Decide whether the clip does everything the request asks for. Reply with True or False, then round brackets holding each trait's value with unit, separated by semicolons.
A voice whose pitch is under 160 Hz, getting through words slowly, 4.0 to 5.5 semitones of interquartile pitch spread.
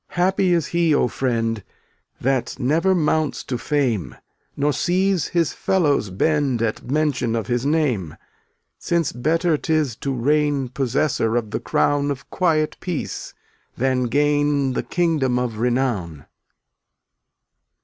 True (140 Hz; 130 wpm; 4.4 semitones)